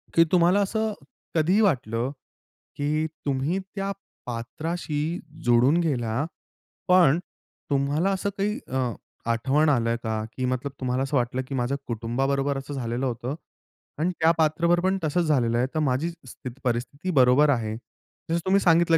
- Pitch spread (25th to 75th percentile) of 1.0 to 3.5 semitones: No, average, 5.0 semitones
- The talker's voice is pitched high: No, medium, 140 Hz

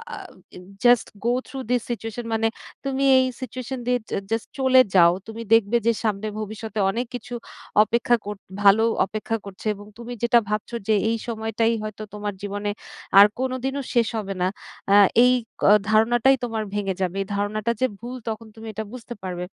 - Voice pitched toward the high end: Yes, high, 225 Hz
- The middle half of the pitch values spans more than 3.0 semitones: No, average, 2.7 semitones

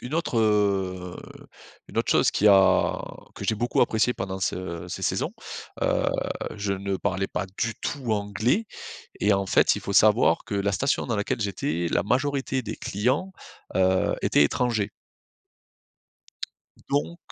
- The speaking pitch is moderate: No, low, 105 Hz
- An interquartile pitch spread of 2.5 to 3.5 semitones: No, average, 4.1 semitones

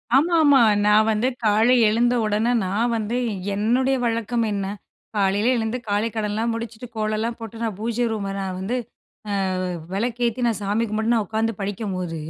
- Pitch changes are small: Yes, narrow, 2.2 semitones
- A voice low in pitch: No, high, 220 Hz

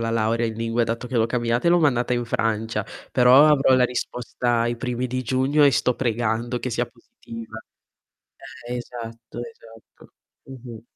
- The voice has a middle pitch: No, low, 120 Hz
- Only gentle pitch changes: Yes, narrow, 1.7 semitones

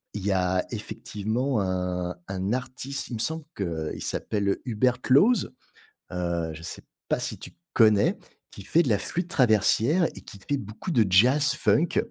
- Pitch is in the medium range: No, low, 110 Hz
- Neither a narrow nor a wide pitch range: No, wide, 6.2 semitones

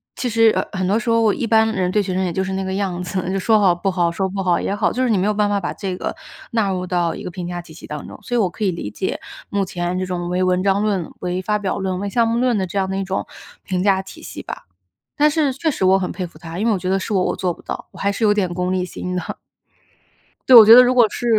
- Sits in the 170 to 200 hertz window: Yes, high, 190 Hz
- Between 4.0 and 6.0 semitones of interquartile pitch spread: No, average, 2.7 semitones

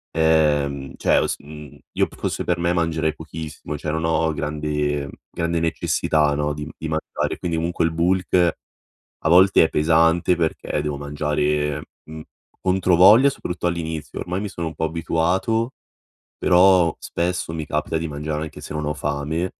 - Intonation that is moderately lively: No, narrow, 2.3 semitones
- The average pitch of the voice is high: No, very low, 80 Hz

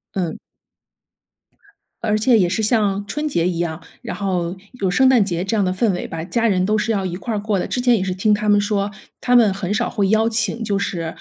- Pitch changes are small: No, average, 3.2 semitones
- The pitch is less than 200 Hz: No, high, 205 Hz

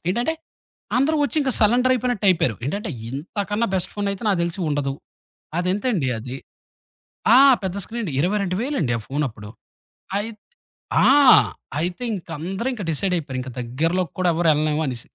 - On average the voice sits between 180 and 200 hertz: Yes, medium, 185 Hz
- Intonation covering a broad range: Yes, wide, 6.0 semitones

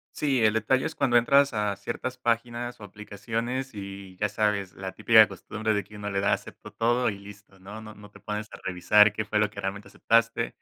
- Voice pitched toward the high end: No, low, 105 Hz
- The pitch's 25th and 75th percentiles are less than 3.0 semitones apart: Yes, narrow, 2.5 semitones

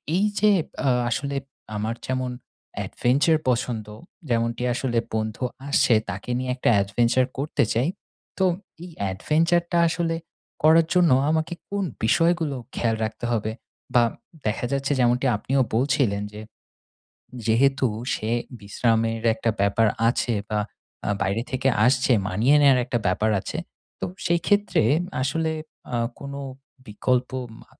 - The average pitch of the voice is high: No, low, 125 Hz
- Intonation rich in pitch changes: No, average, 4.7 semitones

